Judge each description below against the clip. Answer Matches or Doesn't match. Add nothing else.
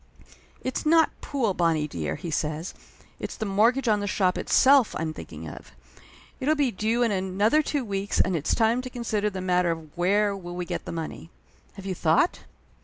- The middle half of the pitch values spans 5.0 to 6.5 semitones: Matches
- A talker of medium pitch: Doesn't match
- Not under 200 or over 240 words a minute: Matches